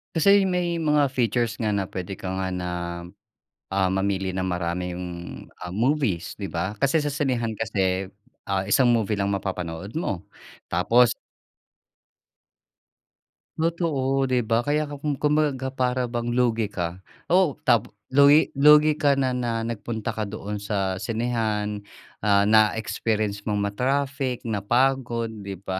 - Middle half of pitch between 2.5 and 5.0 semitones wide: No, wide, 5.6 semitones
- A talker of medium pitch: No, low, 115 Hz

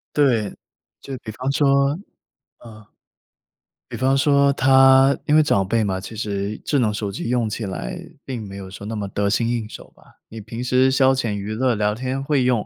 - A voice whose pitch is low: Yes, low, 120 Hz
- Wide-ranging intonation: No, average, 4.2 semitones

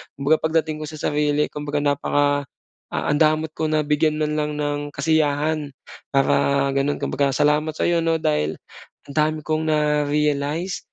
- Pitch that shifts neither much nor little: No, narrow, 1.3 semitones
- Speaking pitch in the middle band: Yes, medium, 150 Hz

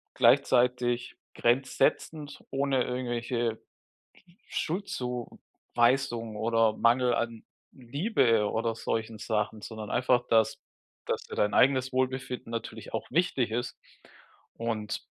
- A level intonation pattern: Yes, narrow, 2.3 semitones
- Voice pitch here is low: Yes, low, 120 Hz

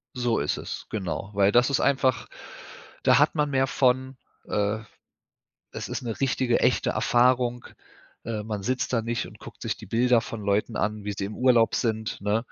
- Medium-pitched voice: No, low, 120 Hz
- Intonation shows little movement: No, average, 3.2 semitones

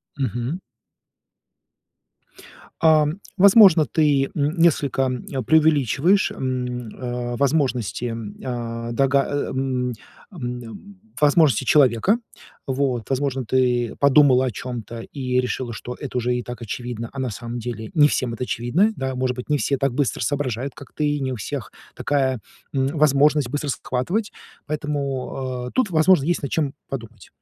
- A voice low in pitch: Yes, low, 130 Hz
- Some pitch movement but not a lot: Yes, average, 3.1 semitones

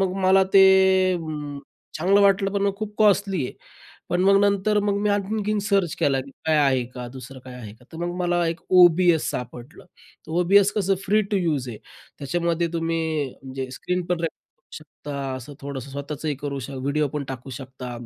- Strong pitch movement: Yes, wide, 5.7 semitones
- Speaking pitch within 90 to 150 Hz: No, medium, 165 Hz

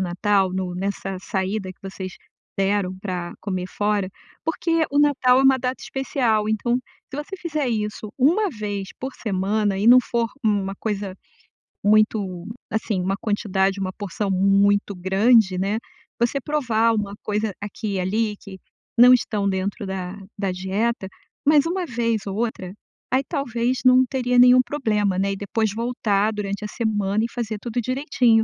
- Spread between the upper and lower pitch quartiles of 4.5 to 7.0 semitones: No, average, 3.8 semitones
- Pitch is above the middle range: Yes, high, 210 Hz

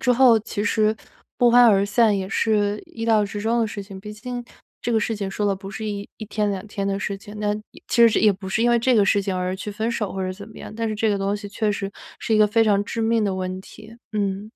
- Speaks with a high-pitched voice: Yes, high, 210 Hz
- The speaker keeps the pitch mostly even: Yes, narrow, 2.1 semitones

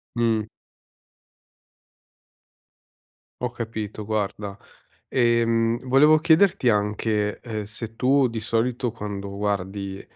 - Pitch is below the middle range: Yes, low, 115 Hz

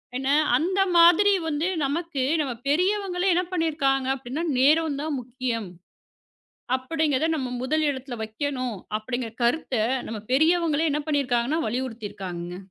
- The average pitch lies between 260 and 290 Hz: Yes, very high, 275 Hz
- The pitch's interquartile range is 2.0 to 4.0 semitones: No, average, 4.4 semitones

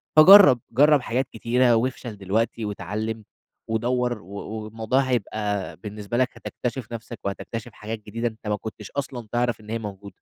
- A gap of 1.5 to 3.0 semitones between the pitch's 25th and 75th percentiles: Yes, narrow, 2.6 semitones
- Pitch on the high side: No, low, 115 Hz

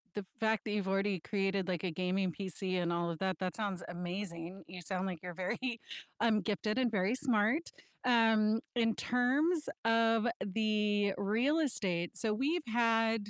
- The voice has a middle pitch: No, high, 210 Hz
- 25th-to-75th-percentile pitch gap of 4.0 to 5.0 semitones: No, average, 3.5 semitones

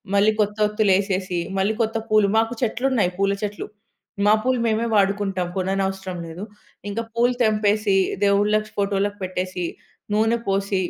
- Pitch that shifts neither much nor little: No, narrow, 2.0 semitones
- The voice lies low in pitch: No, high, 205 Hz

